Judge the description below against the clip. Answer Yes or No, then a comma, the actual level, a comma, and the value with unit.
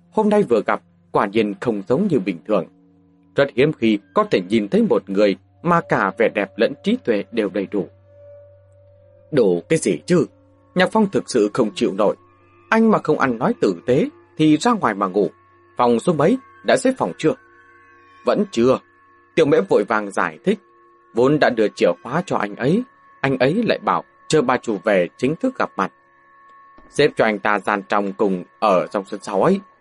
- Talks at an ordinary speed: Yes, average, 200 wpm